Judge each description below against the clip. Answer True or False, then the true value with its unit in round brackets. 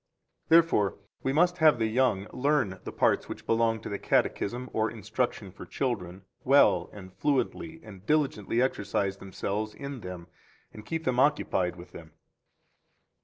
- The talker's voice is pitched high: False (115 Hz)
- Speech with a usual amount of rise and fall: False (5.8 semitones)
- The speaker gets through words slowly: False (155 wpm)